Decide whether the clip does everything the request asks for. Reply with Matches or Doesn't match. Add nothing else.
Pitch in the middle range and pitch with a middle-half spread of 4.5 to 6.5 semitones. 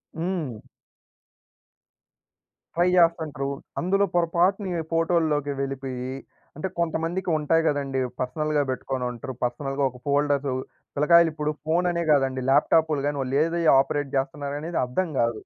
Doesn't match